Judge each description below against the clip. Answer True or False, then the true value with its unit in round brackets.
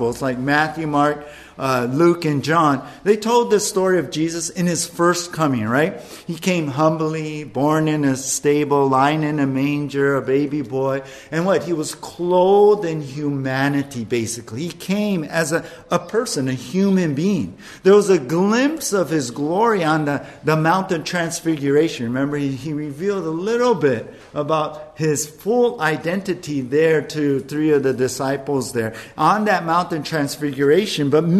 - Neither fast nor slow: True (160 wpm)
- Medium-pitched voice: True (155 Hz)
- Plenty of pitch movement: False (3.7 semitones)